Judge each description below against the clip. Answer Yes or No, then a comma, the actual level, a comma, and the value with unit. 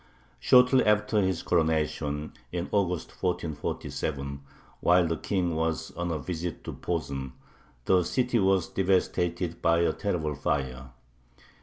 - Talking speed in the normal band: No, slow, 125 wpm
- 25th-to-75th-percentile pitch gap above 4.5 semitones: No, average, 3.3 semitones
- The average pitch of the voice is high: No, very low, 85 Hz